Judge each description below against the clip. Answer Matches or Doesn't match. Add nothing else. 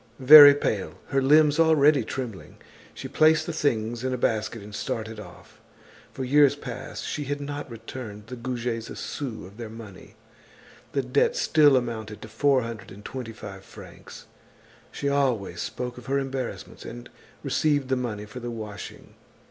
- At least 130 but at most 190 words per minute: Matches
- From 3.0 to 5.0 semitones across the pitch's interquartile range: Matches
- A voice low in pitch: Matches